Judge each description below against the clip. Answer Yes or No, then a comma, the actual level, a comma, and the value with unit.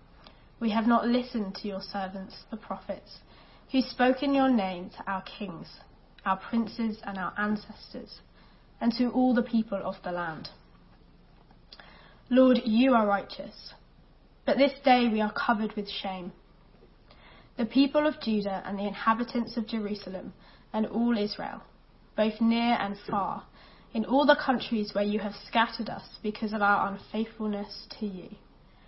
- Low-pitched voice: No, high, 220 Hz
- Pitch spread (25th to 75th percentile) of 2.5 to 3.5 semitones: Yes, average, 2.9 semitones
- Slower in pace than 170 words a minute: Yes, average, 150 wpm